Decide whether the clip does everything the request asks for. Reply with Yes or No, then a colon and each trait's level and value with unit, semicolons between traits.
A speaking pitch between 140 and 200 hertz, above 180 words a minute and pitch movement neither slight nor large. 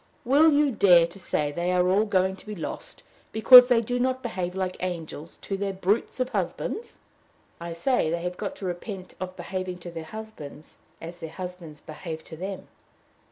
Yes: medium, 185 Hz; average, 190 wpm; average, 4.2 semitones